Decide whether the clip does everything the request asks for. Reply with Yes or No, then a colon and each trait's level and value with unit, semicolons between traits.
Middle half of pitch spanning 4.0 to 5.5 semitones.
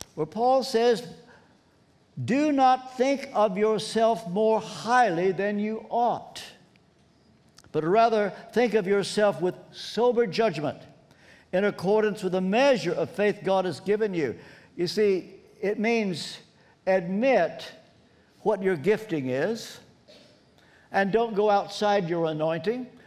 No: average, 3.3 semitones